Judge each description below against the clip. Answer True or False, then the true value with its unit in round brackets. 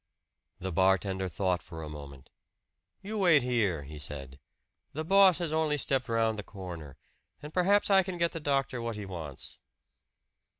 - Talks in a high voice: False (110 Hz)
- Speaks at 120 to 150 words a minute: False (165 wpm)